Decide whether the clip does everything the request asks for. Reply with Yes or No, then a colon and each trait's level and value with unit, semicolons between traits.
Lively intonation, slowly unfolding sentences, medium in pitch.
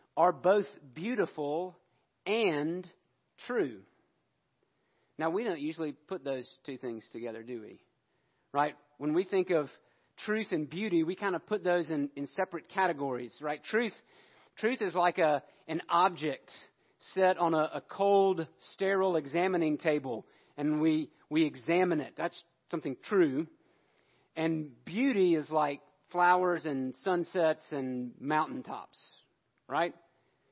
No: average, 3.9 semitones; slow, 130 wpm; medium, 160 Hz